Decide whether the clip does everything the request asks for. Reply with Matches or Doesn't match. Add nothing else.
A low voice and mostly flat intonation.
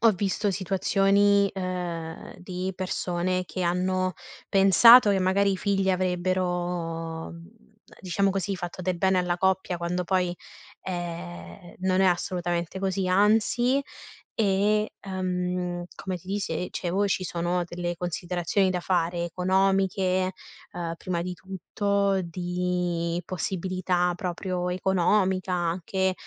Doesn't match